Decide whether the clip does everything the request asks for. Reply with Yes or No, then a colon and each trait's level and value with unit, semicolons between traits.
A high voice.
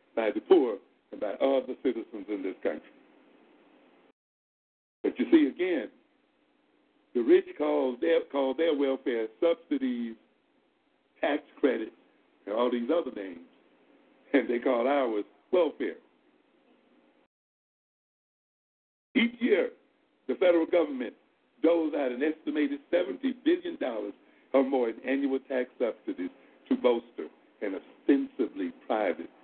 Yes: very high, 275 Hz